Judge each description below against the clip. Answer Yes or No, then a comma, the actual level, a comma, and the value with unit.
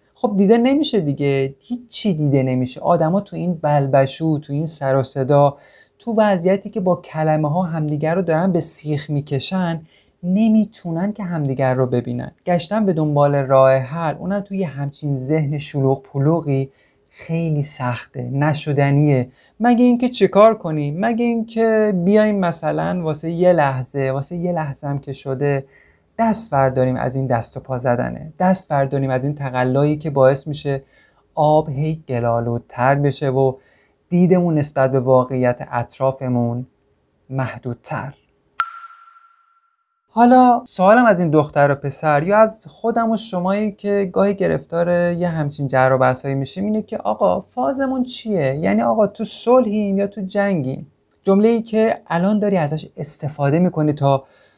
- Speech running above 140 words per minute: Yes, average, 150 wpm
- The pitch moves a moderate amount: No, wide, 6.5 semitones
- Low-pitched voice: No, medium, 155 Hz